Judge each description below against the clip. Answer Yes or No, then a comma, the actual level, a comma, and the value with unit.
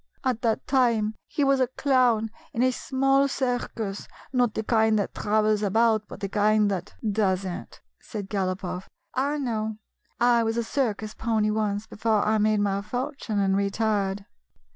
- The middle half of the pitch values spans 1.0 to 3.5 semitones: Yes, average, 3.0 semitones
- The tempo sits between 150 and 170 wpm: No, average, 180 wpm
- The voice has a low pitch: No, high, 220 Hz